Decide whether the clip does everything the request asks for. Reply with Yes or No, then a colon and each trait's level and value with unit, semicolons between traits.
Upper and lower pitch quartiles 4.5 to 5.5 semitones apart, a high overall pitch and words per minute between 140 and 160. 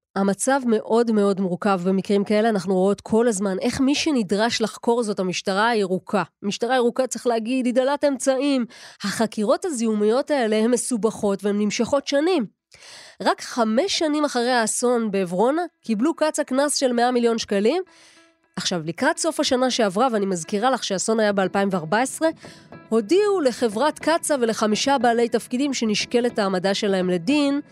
Yes: average, 5.0 semitones; high, 235 Hz; average, 145 wpm